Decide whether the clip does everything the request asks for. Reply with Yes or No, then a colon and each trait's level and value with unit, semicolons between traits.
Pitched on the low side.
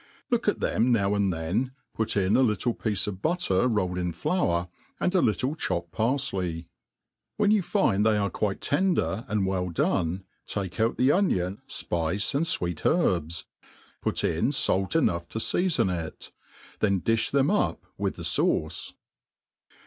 Yes: low, 105 Hz